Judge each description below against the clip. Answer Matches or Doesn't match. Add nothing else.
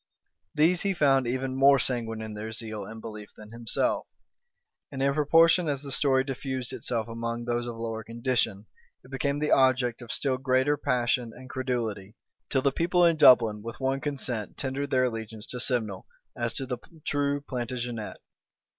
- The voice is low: Matches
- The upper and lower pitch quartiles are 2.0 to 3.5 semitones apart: Matches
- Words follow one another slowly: Doesn't match